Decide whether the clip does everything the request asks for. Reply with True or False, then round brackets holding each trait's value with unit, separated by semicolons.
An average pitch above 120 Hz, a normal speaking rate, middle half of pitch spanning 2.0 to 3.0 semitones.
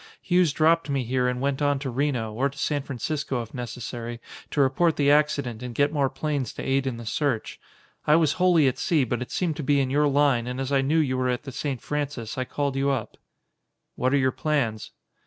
False (135 Hz; 235 wpm; 2.7 semitones)